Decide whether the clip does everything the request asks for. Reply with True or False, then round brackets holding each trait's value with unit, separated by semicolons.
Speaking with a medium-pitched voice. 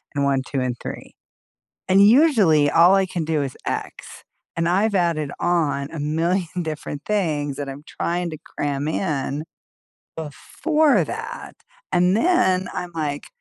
True (165 Hz)